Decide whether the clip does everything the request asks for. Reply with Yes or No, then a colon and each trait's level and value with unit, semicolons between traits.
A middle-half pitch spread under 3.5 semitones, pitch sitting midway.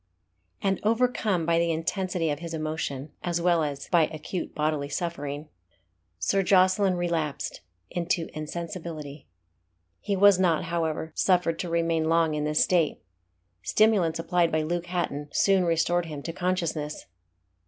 Yes: narrow, 2.5 semitones; medium, 165 Hz